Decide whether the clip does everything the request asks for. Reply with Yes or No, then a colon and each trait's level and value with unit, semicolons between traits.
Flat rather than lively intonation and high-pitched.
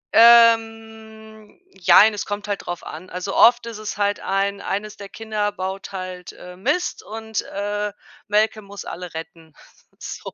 Yes: narrow, 2.3 semitones; high, 205 Hz